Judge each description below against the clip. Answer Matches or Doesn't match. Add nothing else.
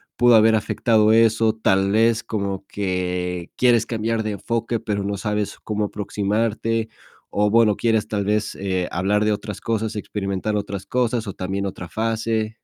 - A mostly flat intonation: Matches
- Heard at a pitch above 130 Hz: Doesn't match